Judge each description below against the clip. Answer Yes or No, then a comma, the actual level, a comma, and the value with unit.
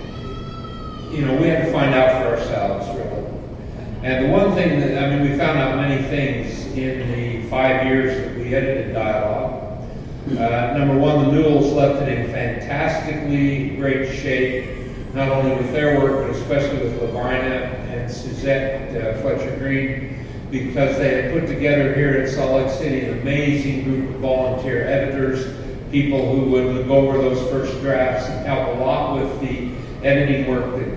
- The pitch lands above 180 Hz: No, low, 135 Hz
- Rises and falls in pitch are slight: Yes, narrow, 1.4 semitones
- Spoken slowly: No, average, 170 wpm